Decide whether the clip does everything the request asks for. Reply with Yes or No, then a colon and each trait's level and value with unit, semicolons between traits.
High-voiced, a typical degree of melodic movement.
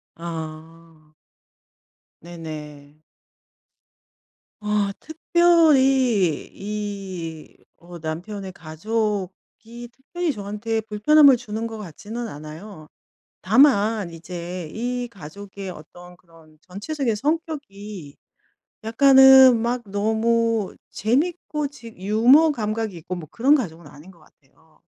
No: high, 210 Hz; wide, 6.0 semitones